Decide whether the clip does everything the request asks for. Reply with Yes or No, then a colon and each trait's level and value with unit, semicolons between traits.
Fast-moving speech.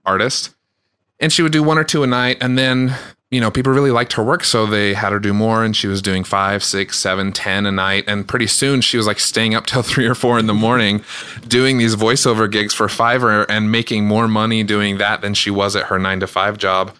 Yes: fast, 250 wpm